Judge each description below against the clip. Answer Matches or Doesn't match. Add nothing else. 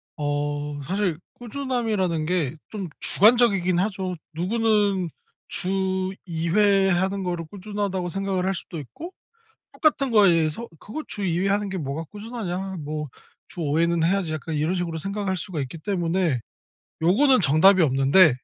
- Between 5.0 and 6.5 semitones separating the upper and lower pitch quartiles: Doesn't match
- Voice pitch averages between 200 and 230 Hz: Doesn't match